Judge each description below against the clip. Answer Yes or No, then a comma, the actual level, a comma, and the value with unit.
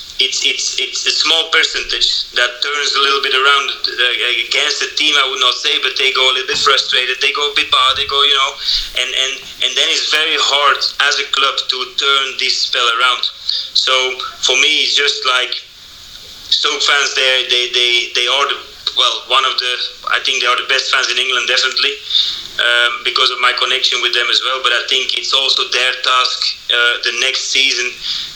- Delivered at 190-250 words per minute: Yes, fast, 205 wpm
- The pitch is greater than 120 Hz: Yes, low, 135 Hz